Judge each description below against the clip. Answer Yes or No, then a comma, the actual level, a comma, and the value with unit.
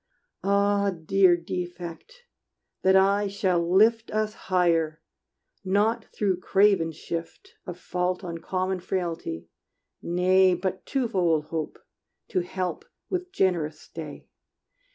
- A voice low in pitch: No, medium, 185 Hz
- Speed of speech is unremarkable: No, slow, 110 wpm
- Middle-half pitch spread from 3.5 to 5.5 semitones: No, average, 2.8 semitones